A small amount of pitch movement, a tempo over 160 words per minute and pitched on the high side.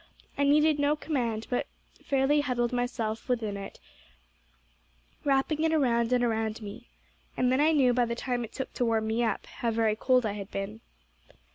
No: average, 3.5 semitones; average, 180 wpm; high, 245 Hz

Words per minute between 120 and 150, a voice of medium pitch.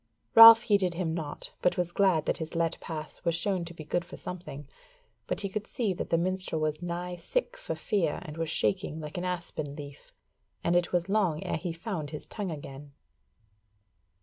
No: average, 200 wpm; medium, 170 Hz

